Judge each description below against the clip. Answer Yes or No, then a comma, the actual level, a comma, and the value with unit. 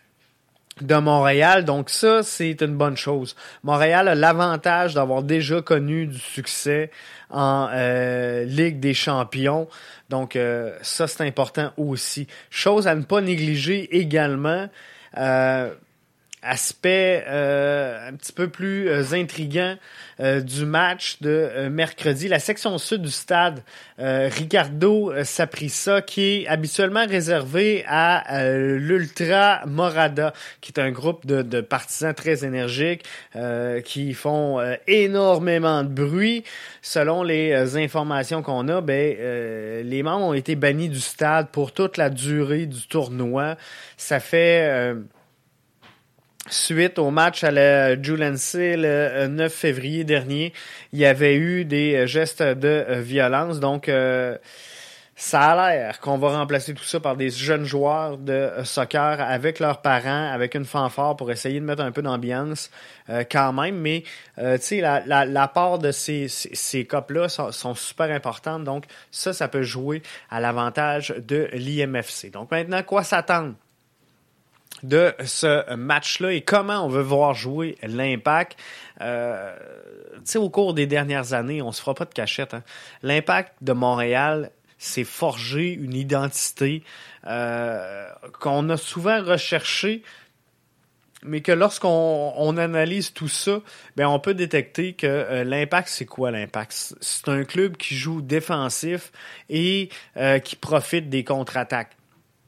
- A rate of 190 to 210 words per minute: No, slow, 145 wpm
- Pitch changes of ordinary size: Yes, average, 3.7 semitones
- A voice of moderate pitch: Yes, medium, 150 Hz